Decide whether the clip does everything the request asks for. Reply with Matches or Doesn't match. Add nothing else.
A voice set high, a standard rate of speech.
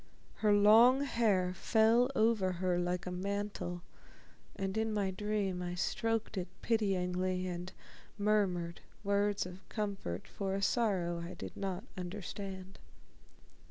Doesn't match